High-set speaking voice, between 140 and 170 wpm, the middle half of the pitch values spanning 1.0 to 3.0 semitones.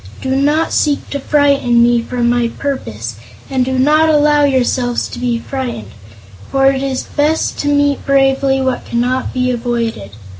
Yes: very high, 265 Hz; average, 160 wpm; average, 2.7 semitones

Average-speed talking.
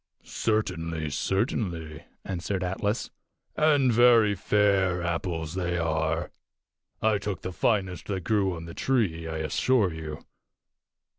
No: slow, 120 wpm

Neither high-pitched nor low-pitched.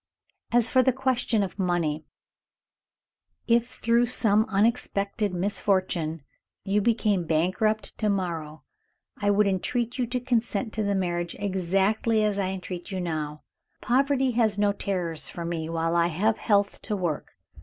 No: high, 200 Hz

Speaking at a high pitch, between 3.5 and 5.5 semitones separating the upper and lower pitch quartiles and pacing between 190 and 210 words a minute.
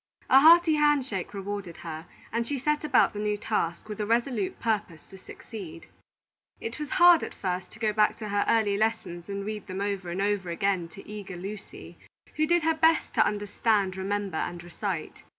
Yes: high, 205 Hz; average, 3.8 semitones; average, 195 wpm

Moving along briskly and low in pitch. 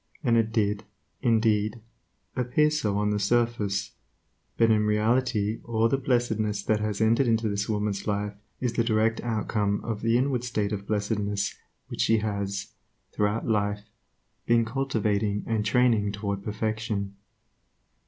No: average, 145 wpm; low, 110 Hz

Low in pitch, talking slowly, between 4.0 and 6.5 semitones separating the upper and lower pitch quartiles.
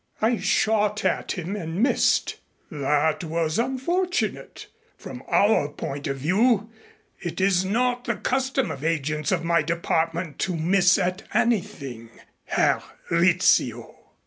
No: medium, 180 Hz; slow, 125 wpm; wide, 5.5 semitones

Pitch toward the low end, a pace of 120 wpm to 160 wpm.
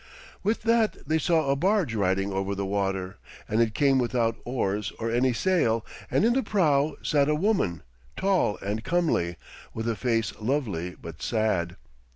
No: low, 115 Hz; average, 170 wpm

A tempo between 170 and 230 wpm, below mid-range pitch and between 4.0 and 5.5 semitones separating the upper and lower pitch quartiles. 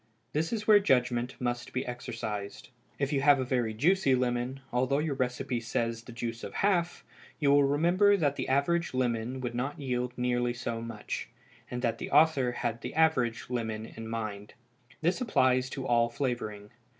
No: average, 175 wpm; low, 125 Hz; average, 3.2 semitones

